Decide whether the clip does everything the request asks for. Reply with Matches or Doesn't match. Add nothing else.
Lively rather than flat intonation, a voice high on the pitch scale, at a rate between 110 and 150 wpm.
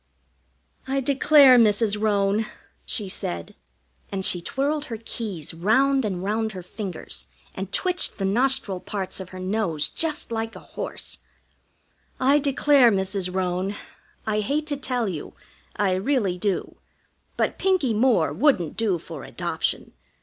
Matches